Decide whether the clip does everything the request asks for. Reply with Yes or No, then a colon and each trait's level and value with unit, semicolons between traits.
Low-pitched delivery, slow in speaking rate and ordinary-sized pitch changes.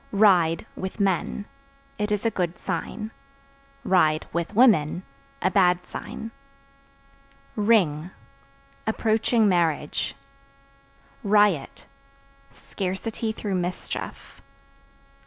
No: high, 190 Hz; slow, 80 wpm; average, 3.8 semitones